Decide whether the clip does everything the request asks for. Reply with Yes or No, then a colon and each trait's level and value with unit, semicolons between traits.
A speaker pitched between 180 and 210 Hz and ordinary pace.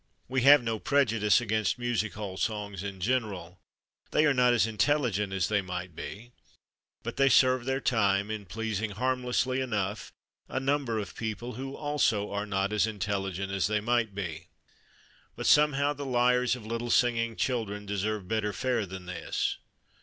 No: low, 110 Hz; average, 165 wpm